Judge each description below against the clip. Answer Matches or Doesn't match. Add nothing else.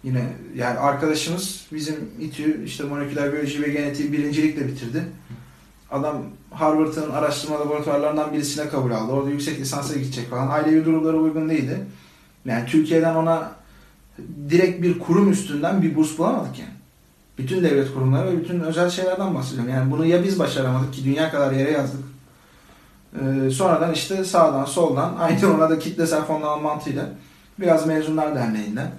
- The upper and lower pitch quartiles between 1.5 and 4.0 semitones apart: Matches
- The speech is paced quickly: Matches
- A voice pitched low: Doesn't match